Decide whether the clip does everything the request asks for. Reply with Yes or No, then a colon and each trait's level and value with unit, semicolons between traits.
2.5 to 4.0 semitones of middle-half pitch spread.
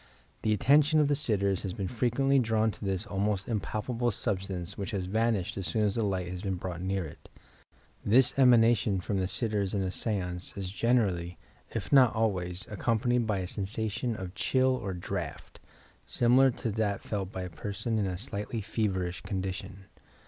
Yes: average, 3.5 semitones